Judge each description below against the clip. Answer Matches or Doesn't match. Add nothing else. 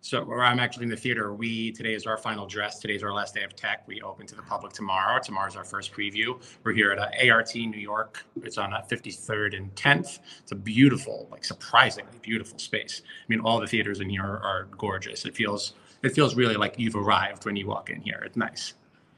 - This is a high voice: Doesn't match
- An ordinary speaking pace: Doesn't match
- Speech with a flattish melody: Matches